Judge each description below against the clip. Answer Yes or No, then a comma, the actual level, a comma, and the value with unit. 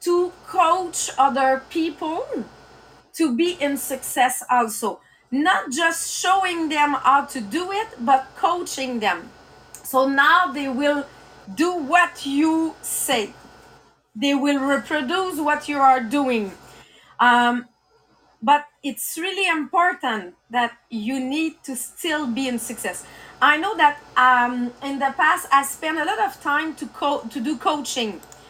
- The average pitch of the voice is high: Yes, very high, 285 Hz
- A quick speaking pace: No, average, 140 wpm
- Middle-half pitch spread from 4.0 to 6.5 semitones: Yes, average, 4.3 semitones